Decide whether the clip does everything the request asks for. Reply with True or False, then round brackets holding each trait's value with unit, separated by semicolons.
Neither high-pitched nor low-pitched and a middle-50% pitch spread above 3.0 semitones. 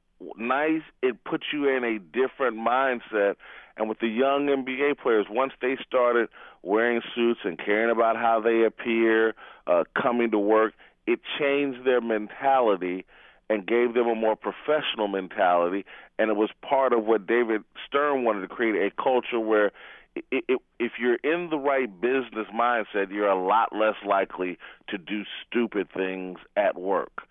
False (115 Hz; 3.4 semitones)